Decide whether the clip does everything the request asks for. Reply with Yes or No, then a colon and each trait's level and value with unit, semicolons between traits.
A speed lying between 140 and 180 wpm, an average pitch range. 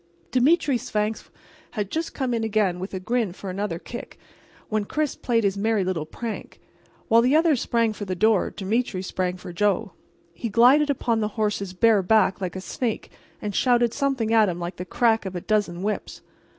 No: average, 190 wpm; average, 3.9 semitones